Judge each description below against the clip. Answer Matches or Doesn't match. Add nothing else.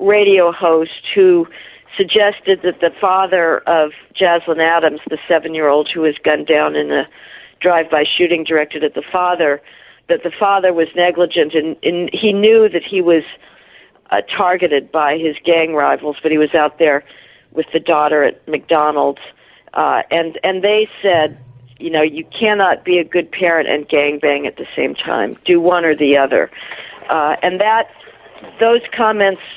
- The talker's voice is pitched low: Doesn't match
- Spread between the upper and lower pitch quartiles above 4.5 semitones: Doesn't match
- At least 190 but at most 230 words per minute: Doesn't match